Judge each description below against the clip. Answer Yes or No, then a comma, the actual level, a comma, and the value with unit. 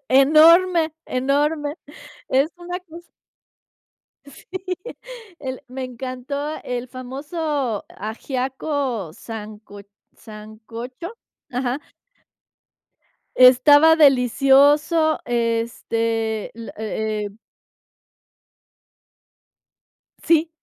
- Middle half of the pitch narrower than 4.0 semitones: No, average, 4.7 semitones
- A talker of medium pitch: No, very high, 260 Hz